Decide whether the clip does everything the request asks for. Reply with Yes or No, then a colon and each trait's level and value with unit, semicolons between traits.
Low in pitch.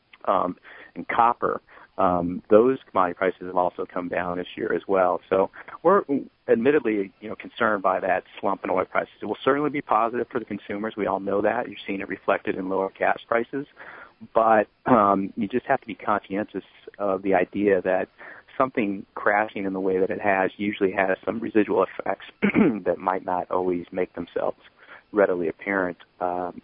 Yes: very low, 95 Hz